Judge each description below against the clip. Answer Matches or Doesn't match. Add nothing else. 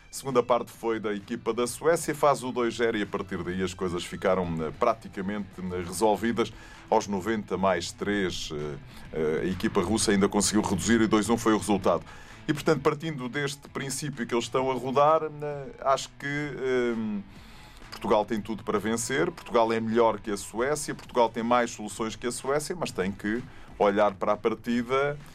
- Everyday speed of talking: Matches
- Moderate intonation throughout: Matches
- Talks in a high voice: Doesn't match